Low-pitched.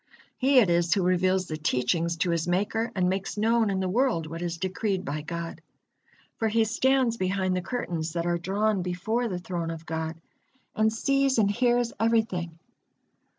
No: medium, 185 Hz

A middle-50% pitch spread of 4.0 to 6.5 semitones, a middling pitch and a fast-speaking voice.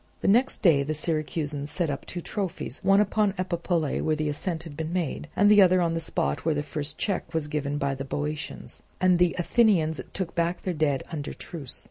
No: average, 3.6 semitones; medium, 160 Hz; fast, 210 wpm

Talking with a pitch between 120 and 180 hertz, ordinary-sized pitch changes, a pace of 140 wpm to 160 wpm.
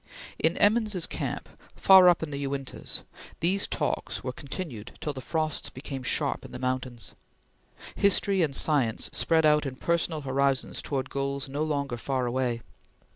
Yes: medium, 140 Hz; average, 3.7 semitones; average, 155 wpm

